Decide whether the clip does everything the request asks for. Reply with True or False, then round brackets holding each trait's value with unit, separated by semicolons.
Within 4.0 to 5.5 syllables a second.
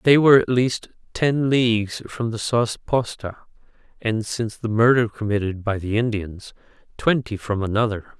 True (4.8 syllables/s)